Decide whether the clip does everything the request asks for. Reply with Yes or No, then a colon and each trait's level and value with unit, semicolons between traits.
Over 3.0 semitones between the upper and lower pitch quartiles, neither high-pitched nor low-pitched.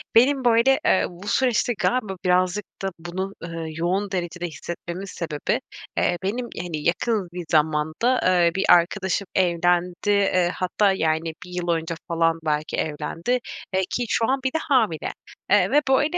Yes: average, 3.7 semitones; medium, 180 Hz